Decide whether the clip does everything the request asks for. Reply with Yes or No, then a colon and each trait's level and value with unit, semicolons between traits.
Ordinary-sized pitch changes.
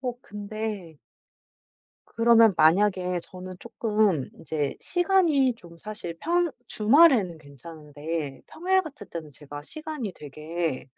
No: wide, 7.3 semitones